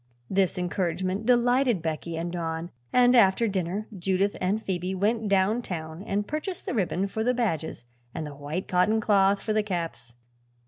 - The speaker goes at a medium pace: Yes, average, 165 wpm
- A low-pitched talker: No, high, 190 Hz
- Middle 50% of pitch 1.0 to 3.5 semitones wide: No, average, 4.2 semitones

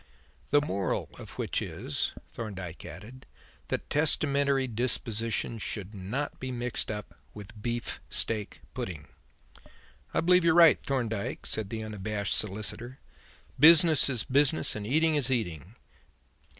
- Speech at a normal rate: No, slow, 125 wpm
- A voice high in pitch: No, low, 115 Hz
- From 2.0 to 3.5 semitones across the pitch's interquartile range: No, average, 5.0 semitones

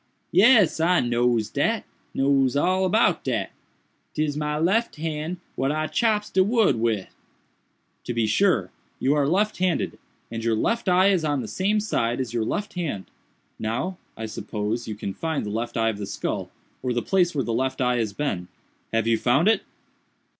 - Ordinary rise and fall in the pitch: No, wide, 7.9 semitones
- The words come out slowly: No, average, 180 wpm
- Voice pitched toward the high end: No, medium, 140 Hz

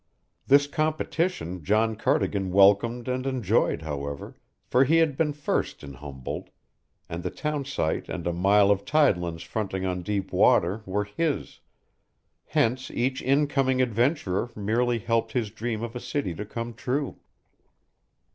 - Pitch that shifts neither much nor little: No, wide, 5.8 semitones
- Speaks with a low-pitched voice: Yes, low, 115 Hz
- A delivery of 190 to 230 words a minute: No, average, 140 wpm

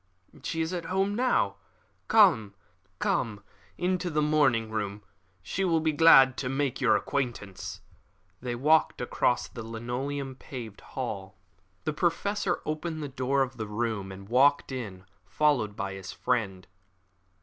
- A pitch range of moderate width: No, wide, 6.1 semitones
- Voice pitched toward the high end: No, low, 130 Hz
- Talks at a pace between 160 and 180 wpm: No, average, 140 wpm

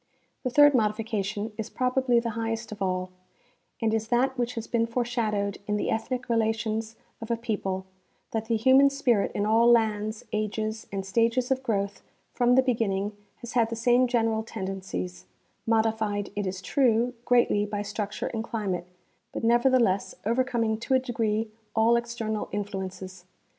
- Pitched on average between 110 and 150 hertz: No, high, 225 Hz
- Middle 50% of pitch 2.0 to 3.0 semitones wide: Yes, narrow, 2.5 semitones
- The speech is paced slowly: No, average, 160 wpm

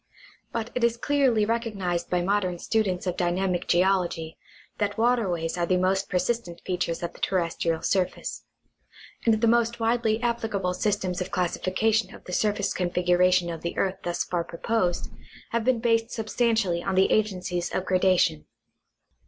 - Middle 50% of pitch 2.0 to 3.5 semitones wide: No, average, 3.9 semitones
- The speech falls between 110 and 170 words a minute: Yes, average, 160 wpm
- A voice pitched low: No, high, 190 Hz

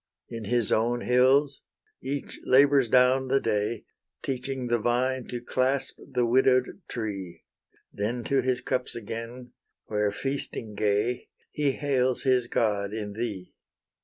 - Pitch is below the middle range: Yes, low, 125 Hz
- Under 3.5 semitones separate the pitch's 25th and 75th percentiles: Yes, average, 2.9 semitones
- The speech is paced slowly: Yes, slow, 130 wpm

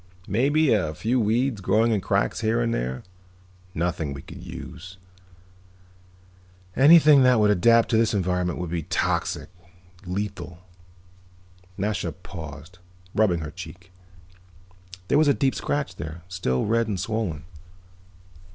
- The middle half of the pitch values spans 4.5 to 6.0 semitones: Yes, average, 5.1 semitones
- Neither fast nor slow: No, slow, 130 wpm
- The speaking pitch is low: Yes, low, 100 Hz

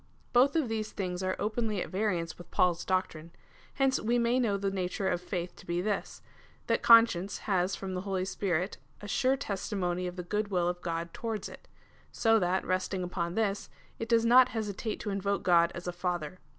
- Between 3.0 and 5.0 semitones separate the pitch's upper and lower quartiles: Yes, average, 3.6 semitones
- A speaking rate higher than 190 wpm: Yes, average, 200 wpm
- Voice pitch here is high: Yes, high, 195 Hz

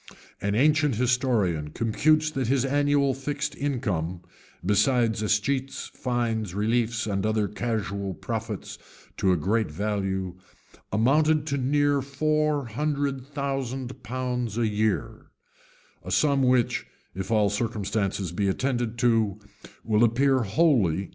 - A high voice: No, low, 120 Hz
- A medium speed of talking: No, slow, 120 wpm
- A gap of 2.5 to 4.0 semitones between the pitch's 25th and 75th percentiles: No, average, 4.9 semitones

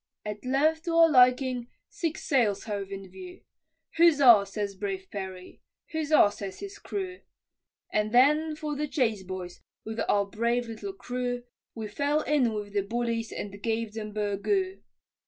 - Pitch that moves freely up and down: Yes, wide, 6.6 semitones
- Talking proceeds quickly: No, average, 155 wpm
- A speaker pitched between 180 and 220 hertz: No, high, 235 Hz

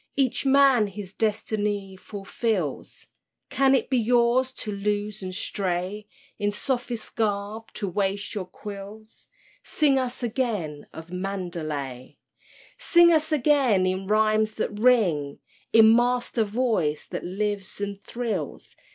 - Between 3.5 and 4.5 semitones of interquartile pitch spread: Yes, average, 3.9 semitones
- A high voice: Yes, high, 210 Hz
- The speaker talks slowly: Yes, slow, 125 wpm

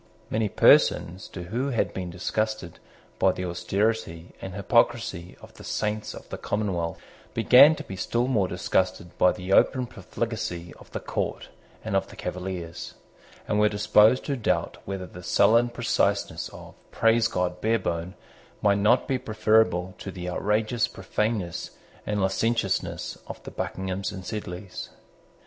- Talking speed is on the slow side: No, average, 150 wpm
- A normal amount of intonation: Yes, average, 3.6 semitones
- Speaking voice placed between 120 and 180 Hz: No, low, 100 Hz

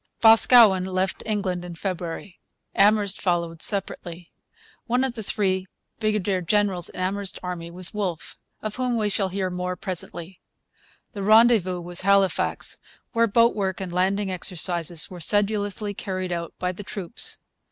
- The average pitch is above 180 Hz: Yes, high, 190 Hz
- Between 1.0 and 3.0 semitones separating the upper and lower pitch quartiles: Yes, narrow, 2.6 semitones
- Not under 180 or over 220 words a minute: No, average, 145 wpm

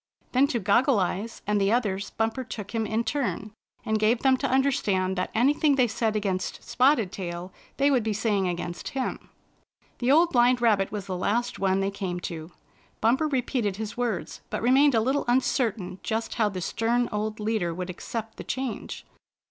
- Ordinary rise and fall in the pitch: Yes, average, 4.2 semitones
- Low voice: No, high, 220 Hz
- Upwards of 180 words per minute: Yes, average, 190 wpm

